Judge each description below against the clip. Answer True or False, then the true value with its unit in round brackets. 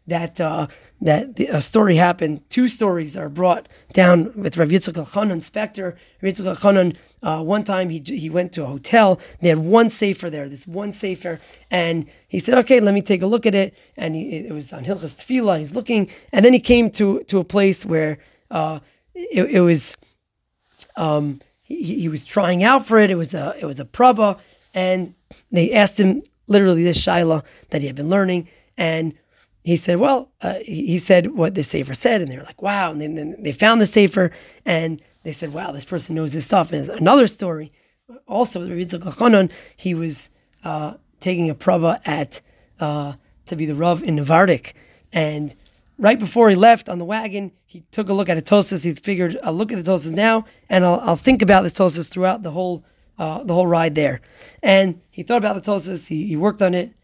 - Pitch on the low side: False (180 Hz)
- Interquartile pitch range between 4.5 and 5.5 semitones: False (3.9 semitones)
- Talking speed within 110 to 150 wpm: False (205 wpm)